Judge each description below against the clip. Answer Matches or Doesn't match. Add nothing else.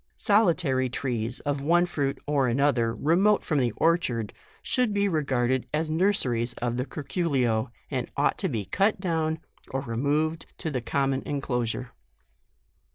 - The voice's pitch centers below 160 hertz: Matches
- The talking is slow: Doesn't match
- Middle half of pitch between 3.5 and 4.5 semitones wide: Doesn't match